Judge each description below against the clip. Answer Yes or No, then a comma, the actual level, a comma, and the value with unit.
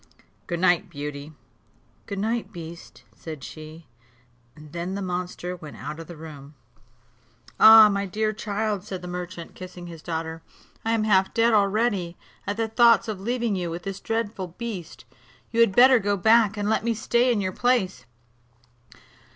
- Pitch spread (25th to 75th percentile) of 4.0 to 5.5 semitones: Yes, average, 4.4 semitones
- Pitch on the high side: Yes, high, 195 Hz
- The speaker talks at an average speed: Yes, average, 165 wpm